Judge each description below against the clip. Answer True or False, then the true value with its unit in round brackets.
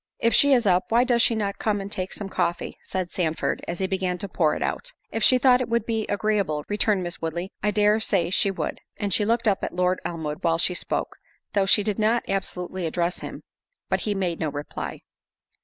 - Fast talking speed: True (225 wpm)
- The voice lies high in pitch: True (195 Hz)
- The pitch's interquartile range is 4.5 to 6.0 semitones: False (3.5 semitones)